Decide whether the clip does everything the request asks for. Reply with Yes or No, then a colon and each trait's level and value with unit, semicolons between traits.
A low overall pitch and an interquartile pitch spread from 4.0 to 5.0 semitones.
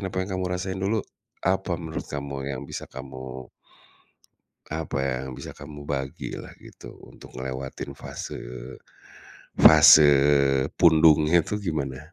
Yes: very low, 75 Hz; average, 4.5 semitones